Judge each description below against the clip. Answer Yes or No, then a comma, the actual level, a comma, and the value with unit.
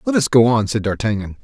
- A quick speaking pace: Yes, fast, 250 wpm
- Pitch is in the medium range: No, low, 115 Hz